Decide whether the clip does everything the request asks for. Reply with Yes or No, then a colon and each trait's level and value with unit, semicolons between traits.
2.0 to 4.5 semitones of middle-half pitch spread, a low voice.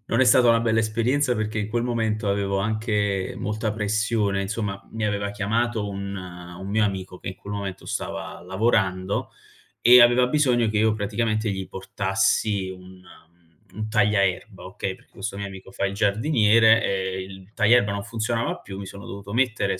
Yes: narrow, 2.5 semitones; low, 105 Hz